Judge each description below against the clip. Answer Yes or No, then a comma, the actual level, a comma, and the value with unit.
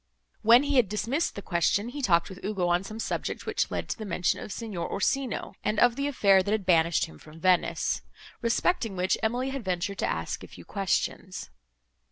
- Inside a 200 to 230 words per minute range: Yes, fast, 205 wpm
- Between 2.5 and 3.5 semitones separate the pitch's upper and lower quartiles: No, average, 4.6 semitones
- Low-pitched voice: No, high, 200 Hz